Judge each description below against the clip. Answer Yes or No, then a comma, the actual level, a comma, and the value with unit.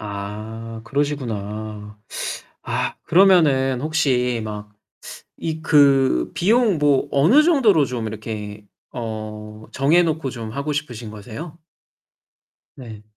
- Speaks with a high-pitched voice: No, low, 125 Hz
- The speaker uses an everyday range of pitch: No, wide, 5.8 semitones